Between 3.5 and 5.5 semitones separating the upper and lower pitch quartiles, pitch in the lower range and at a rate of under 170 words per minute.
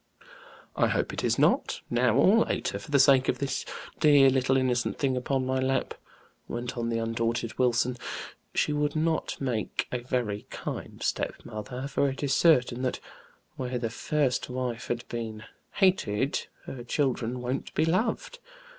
No: narrow, 2.5 semitones; low, 130 Hz; average, 160 wpm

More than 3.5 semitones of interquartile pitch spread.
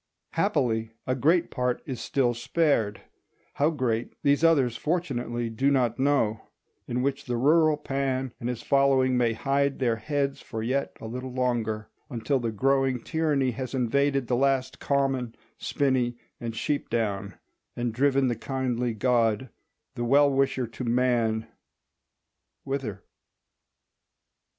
No: average, 2.7 semitones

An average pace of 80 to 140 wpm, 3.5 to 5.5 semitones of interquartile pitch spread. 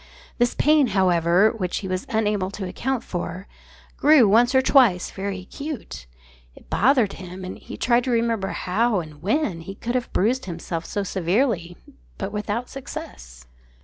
No: average, 160 wpm; average, 4.8 semitones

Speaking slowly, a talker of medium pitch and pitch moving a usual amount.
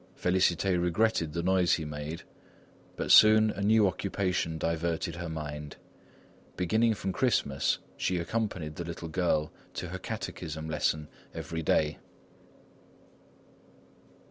No: slow, 115 wpm; very low, 85 Hz; average, 3.3 semitones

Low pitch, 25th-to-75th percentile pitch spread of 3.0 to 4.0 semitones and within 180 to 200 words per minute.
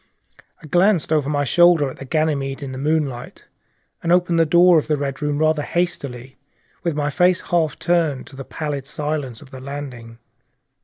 No: medium, 150 Hz; average, 3.3 semitones; average, 190 wpm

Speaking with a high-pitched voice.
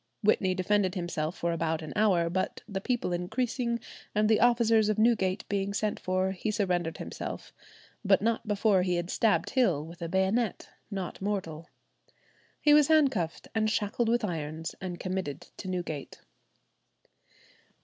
Yes: high, 195 Hz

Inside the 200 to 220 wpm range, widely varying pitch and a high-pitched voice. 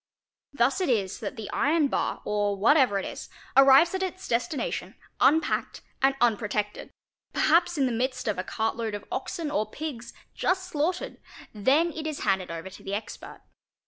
No: average, 170 wpm; wide, 7.0 semitones; very high, 255 Hz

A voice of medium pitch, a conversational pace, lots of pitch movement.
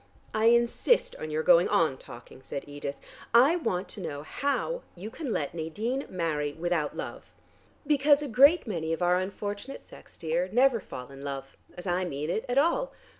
Yes: medium, 180 Hz; average, 180 wpm; wide, 7.9 semitones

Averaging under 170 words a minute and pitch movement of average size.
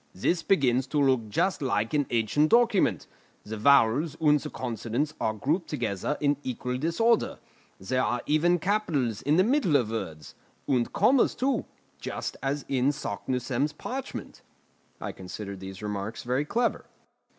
No: average, 150 wpm; wide, 5.9 semitones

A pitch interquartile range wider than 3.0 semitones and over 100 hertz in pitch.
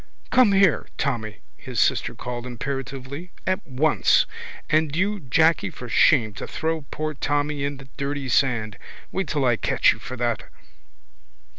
Yes: average, 4.2 semitones; medium, 140 Hz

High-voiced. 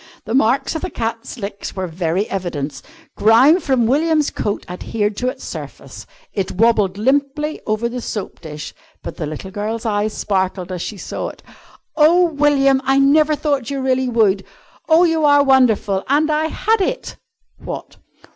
Yes: high, 235 Hz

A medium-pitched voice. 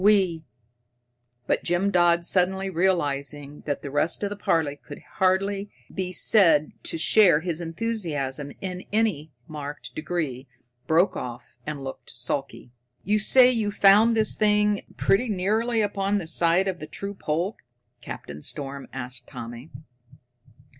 Yes: medium, 170 Hz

